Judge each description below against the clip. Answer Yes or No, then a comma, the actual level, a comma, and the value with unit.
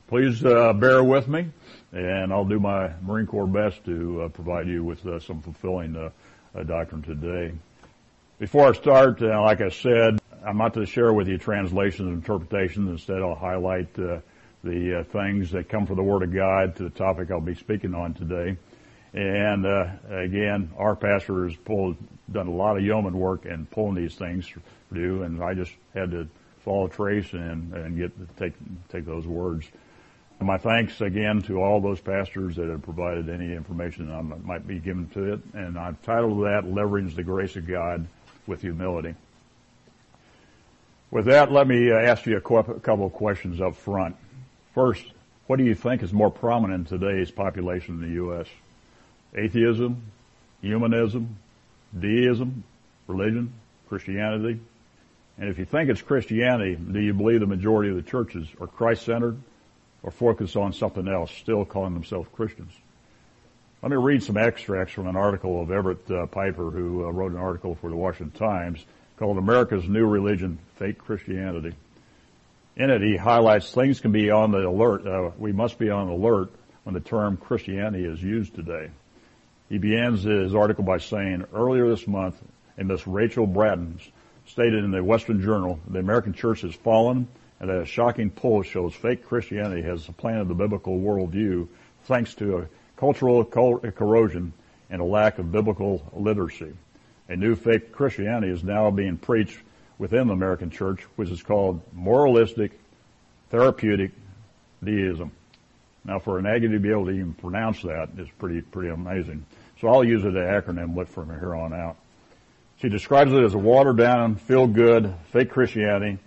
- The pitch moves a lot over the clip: No, average, 3.9 semitones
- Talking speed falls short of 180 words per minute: Yes, average, 170 wpm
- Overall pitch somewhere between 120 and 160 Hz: No, low, 100 Hz